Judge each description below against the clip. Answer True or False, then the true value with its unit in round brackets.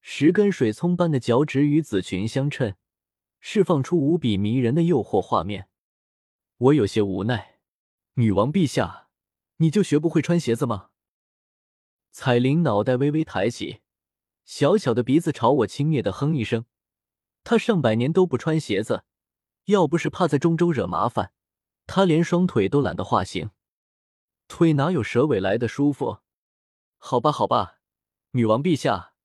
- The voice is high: False (140 Hz)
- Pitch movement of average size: False (7.5 semitones)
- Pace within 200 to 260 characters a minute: True (225 characters per minute)